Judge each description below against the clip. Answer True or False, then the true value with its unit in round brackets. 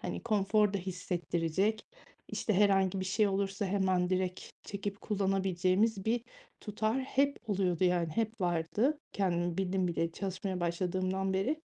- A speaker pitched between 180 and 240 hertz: True (190 Hz)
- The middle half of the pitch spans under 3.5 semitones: True (2.4 semitones)